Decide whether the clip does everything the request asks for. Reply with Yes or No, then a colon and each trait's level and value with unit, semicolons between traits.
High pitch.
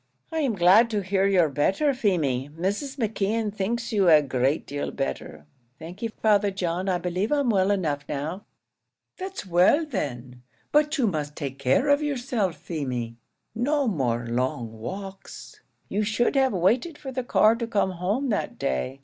Yes: high, 195 Hz